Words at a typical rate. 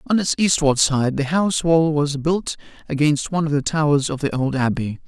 No: fast, 215 wpm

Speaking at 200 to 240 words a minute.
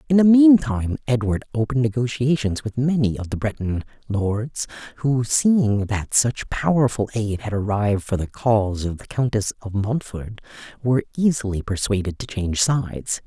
No: average, 155 wpm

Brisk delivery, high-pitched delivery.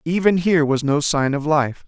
No: fast, 225 wpm; medium, 155 Hz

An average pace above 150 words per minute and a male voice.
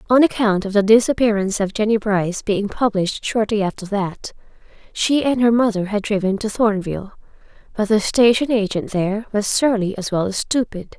No: average, 175 wpm; female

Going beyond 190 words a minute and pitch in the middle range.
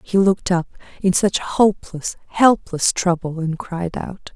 No: average, 150 wpm; medium, 180 Hz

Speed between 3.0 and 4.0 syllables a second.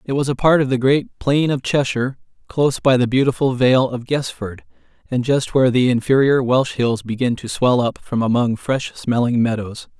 No: 5.1 syllables/s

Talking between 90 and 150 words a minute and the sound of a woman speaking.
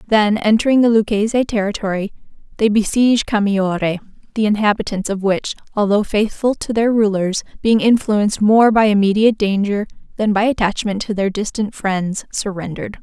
Yes: average, 145 wpm; female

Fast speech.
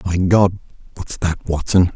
No: average, 155 wpm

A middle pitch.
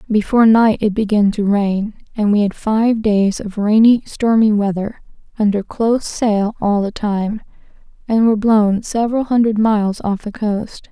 No: high, 215 Hz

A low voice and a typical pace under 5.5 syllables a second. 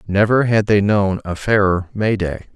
Yes: low, 100 Hz; 4.5 syllables/s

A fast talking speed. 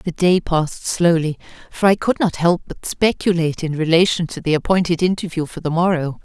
No: average, 190 wpm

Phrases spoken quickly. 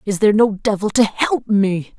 Yes: fast, 210 wpm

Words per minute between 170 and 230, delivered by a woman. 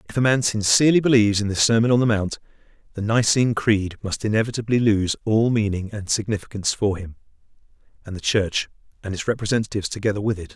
No: average, 180 wpm; male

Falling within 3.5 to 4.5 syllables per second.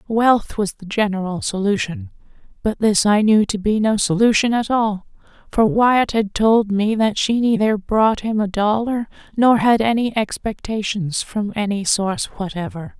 Yes: 4.4 syllables/s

